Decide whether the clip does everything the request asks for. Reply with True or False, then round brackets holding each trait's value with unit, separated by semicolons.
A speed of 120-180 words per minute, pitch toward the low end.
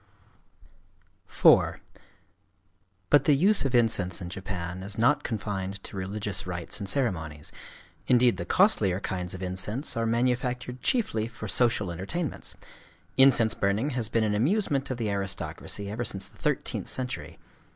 True (140 wpm; 110 Hz)